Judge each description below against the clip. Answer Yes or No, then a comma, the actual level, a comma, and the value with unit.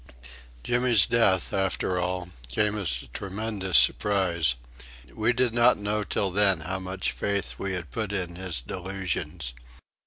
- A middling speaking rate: Yes, average, 145 wpm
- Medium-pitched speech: No, very low, 95 Hz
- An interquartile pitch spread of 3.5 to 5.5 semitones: No, average, 2.8 semitones